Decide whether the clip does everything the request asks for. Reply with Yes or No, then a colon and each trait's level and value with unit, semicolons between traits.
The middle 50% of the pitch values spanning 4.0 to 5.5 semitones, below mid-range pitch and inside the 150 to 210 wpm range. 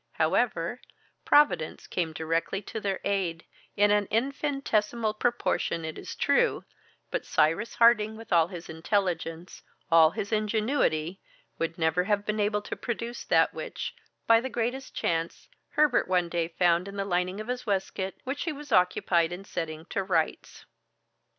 No: average, 5.0 semitones; high, 195 Hz; average, 155 wpm